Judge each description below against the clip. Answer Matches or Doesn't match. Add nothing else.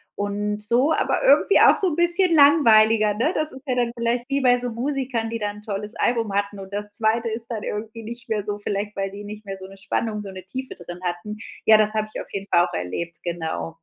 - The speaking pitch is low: Doesn't match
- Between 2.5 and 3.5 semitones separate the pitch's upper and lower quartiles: Matches